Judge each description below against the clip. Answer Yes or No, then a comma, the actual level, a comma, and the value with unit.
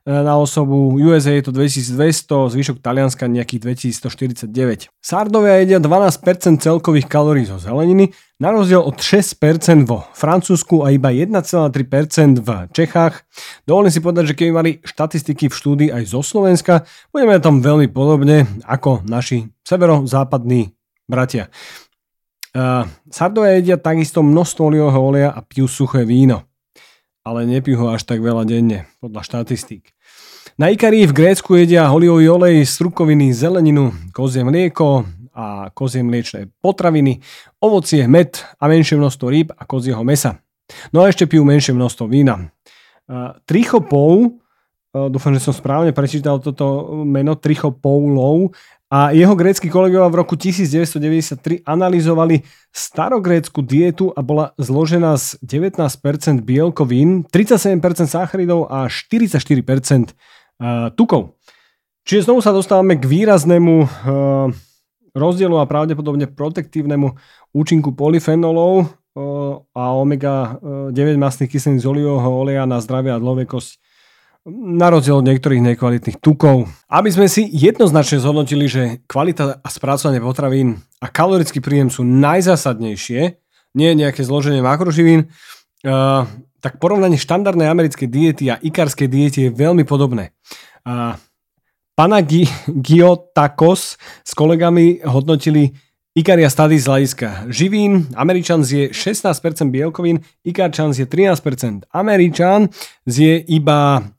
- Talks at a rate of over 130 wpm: No, average, 120 wpm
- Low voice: No, medium, 145 Hz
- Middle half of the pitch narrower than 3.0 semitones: No, average, 4.2 semitones